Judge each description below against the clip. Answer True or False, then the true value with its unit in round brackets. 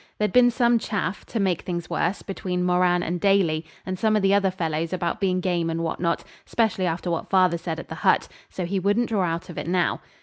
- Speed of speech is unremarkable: False (235 wpm)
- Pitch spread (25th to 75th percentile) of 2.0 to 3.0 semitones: True (2.7 semitones)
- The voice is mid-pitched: True (180 Hz)